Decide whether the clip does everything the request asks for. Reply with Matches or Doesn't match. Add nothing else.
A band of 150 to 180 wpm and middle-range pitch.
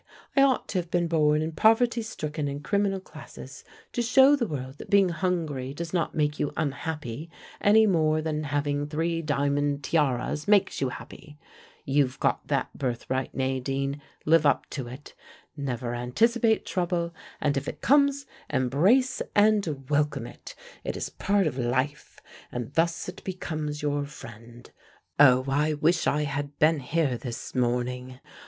Matches